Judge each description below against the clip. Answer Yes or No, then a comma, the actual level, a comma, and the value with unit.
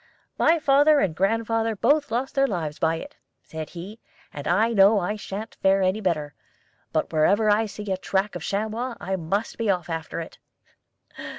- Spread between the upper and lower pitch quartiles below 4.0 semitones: No, average, 4.4 semitones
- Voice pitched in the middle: No, high, 200 Hz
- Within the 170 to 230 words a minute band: Yes, average, 185 wpm